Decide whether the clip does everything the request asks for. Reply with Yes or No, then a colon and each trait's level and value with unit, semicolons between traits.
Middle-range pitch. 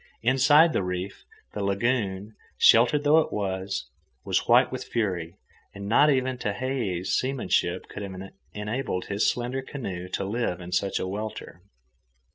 No: low, 105 Hz